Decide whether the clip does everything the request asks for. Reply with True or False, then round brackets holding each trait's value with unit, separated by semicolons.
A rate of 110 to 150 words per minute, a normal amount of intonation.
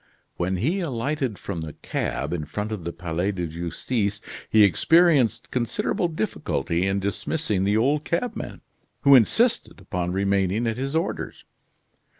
False (145 wpm; 7.1 semitones)